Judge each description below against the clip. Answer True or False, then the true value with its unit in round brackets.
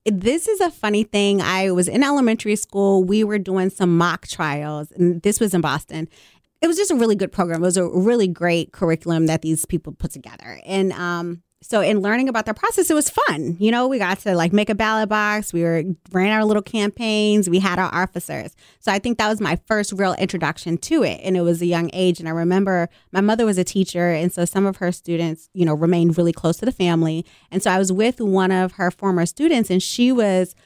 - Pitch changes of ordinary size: True (3.6 semitones)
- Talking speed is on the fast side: True (240 wpm)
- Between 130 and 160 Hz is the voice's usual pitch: False (185 Hz)